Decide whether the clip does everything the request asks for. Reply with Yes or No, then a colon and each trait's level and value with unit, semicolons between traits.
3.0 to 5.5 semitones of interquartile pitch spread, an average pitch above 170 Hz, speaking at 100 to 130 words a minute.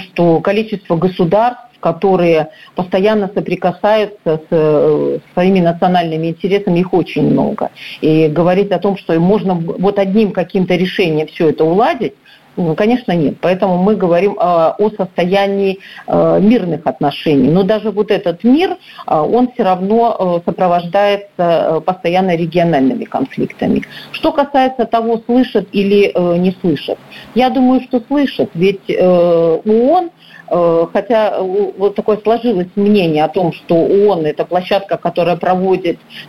Yes: average, 3.6 semitones; high, 190 Hz; average, 120 wpm